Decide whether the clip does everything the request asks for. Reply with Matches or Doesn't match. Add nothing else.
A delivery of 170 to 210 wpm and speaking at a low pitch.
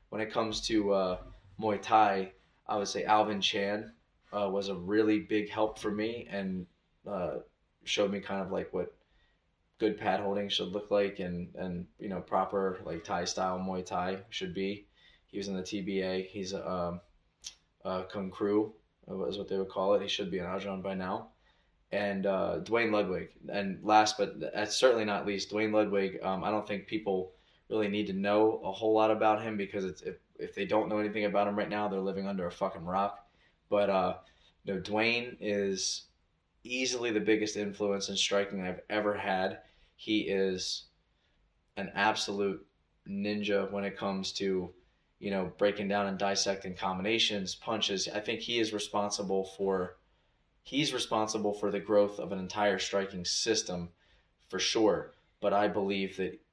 Matches